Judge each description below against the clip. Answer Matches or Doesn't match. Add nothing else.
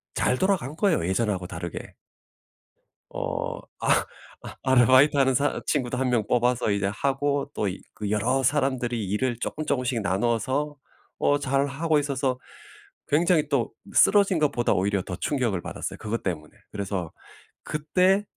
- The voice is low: Matches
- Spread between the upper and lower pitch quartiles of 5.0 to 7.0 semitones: Matches